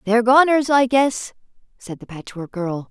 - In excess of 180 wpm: No, average, 165 wpm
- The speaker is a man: No, female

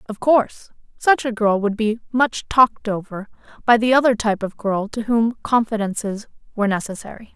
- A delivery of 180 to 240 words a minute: No, average, 170 wpm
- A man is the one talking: No, female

